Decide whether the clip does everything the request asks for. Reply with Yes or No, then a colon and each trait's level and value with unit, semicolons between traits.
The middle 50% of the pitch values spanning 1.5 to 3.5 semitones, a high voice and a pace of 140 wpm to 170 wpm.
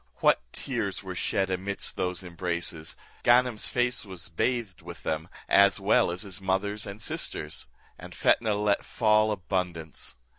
No: average, 3.2 semitones; very low, 95 Hz; average, 145 wpm